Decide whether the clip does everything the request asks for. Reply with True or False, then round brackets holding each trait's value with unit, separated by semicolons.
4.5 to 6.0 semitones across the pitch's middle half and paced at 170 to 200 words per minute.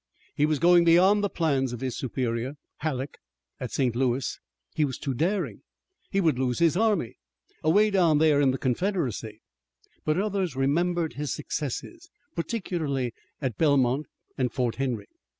False (5.1 semitones; 150 wpm)